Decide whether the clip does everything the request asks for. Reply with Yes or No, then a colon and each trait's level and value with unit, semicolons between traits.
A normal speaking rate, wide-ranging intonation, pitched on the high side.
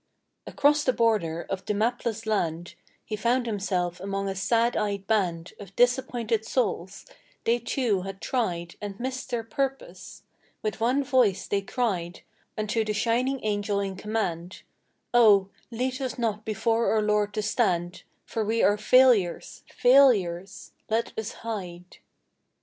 No: average, 145 wpm; average, 3.6 semitones; high, 215 Hz